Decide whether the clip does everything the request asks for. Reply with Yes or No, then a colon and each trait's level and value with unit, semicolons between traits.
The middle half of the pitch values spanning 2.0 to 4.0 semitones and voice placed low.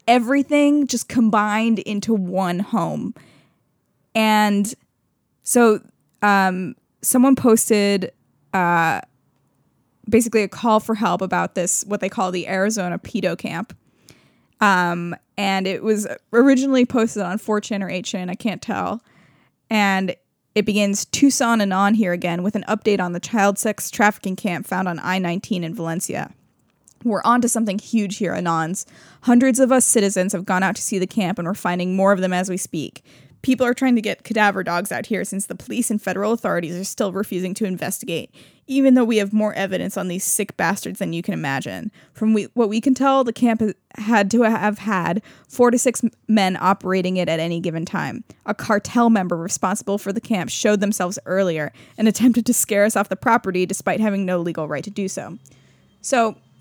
No: average, 3.4 semitones; high, 205 Hz